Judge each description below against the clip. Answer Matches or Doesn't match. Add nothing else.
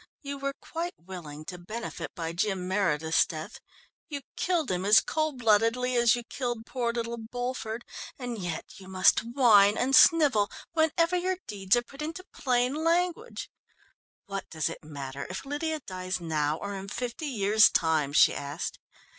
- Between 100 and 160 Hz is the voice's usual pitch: Doesn't match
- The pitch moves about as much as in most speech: Doesn't match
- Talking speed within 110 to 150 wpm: Doesn't match